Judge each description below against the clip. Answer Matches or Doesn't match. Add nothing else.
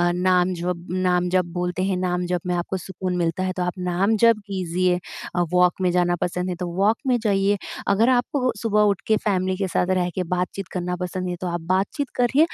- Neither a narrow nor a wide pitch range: Doesn't match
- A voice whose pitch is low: Doesn't match